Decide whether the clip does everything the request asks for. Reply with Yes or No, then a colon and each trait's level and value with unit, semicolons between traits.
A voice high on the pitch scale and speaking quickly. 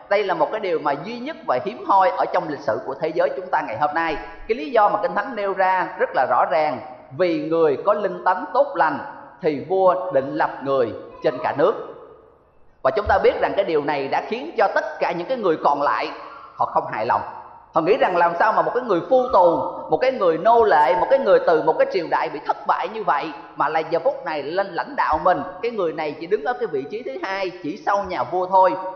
Yes: high, 200 Hz; fast, 260 wpm